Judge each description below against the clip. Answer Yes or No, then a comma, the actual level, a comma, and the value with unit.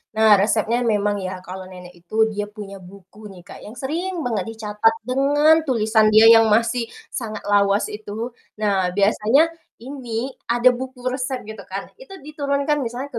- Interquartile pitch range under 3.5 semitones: No, average, 3.8 semitones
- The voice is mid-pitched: No, high, 220 Hz